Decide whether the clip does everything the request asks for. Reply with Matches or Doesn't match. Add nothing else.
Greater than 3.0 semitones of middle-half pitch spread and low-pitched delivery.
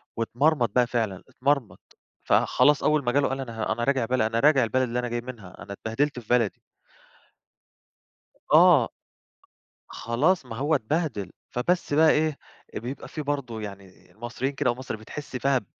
Matches